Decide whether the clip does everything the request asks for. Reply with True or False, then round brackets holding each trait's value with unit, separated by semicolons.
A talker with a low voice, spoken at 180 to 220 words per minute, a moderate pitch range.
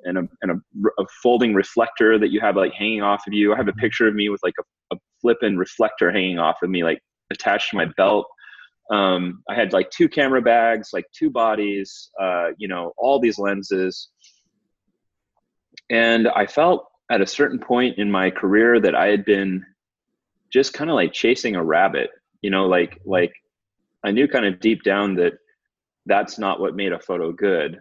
True (105 Hz; 195 wpm; 3.5 semitones)